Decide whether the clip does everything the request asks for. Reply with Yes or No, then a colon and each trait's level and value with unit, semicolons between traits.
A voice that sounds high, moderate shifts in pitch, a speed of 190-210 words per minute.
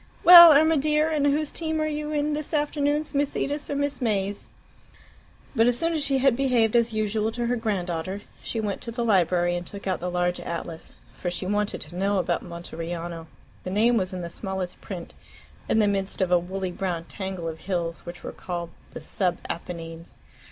No: high, 200 Hz; wide, 7.8 semitones; fast, 205 wpm